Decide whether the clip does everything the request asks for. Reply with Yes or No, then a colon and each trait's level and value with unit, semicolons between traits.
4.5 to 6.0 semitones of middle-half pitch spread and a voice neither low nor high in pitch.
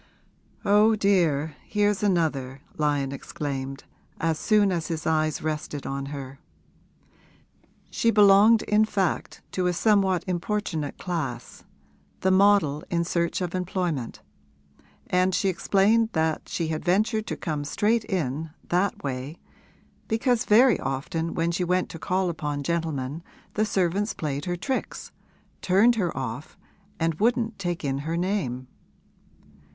Yes: average, 5.1 semitones; medium, 175 Hz